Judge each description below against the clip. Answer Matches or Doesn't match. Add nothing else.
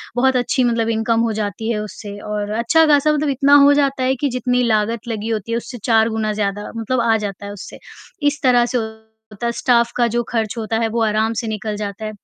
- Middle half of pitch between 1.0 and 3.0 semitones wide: Matches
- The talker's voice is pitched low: Doesn't match